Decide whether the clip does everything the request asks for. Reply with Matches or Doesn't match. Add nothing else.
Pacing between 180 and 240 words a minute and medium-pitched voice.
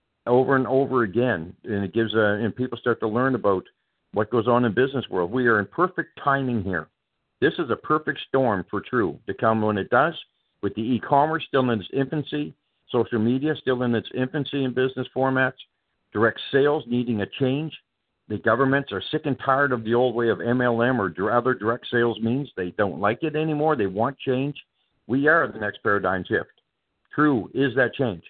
Doesn't match